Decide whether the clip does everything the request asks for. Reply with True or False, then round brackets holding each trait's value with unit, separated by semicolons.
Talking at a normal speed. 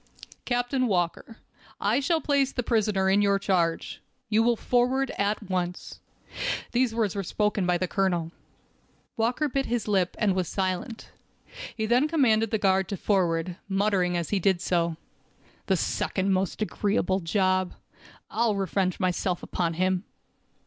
True (150 wpm)